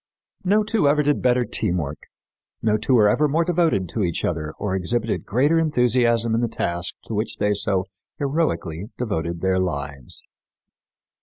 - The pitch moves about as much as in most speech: No, wide, 7.5 semitones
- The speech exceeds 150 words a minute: Yes, average, 160 wpm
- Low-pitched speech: Yes, low, 110 Hz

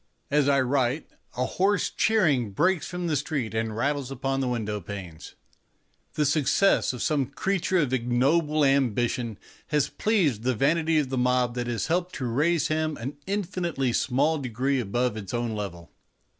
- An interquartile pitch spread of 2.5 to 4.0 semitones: No, average, 4.5 semitones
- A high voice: No, low, 135 Hz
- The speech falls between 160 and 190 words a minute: Yes, average, 165 wpm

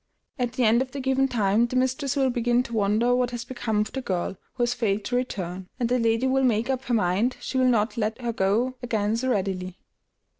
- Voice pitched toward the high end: Yes, high, 240 Hz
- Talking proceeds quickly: Yes, fast, 235 wpm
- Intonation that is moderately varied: Yes, average, 3.2 semitones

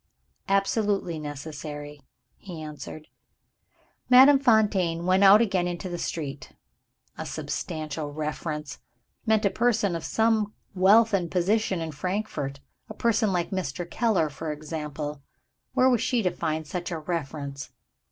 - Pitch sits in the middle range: Yes, medium, 175 Hz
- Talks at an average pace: No, slow, 130 wpm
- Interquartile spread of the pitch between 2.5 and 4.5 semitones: No, average, 5.3 semitones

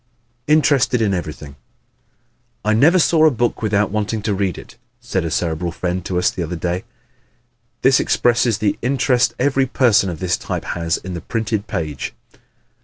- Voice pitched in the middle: No, low, 105 Hz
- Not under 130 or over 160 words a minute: No, average, 175 wpm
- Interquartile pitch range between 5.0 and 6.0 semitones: Yes, wide, 5.6 semitones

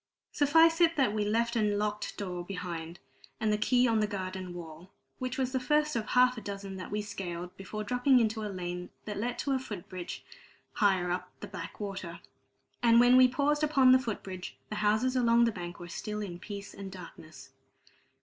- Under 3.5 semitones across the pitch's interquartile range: No, average, 5.2 semitones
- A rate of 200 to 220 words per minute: Yes, fast, 205 wpm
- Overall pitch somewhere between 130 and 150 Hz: No, high, 210 Hz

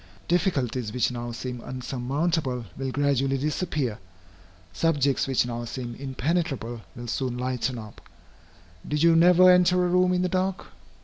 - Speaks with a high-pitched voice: No, low, 135 Hz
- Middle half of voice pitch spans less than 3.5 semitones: No, wide, 5.5 semitones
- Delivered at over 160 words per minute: No, average, 140 wpm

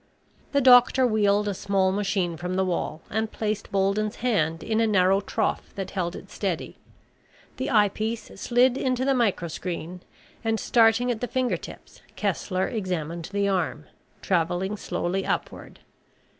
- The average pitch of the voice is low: No, high, 200 Hz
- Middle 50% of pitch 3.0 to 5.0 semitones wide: Yes, average, 3.6 semitones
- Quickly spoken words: No, average, 145 wpm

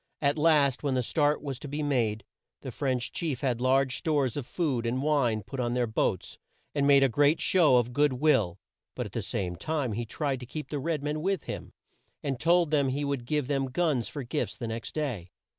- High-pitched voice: No, medium, 140 Hz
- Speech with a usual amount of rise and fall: Yes, average, 3.5 semitones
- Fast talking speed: Yes, fast, 225 wpm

